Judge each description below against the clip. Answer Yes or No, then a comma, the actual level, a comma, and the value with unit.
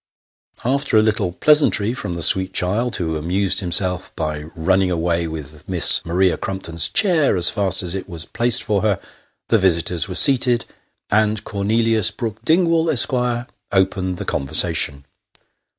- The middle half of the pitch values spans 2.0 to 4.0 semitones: No, average, 4.9 semitones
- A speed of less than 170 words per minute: Yes, average, 150 wpm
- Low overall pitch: Yes, very low, 95 Hz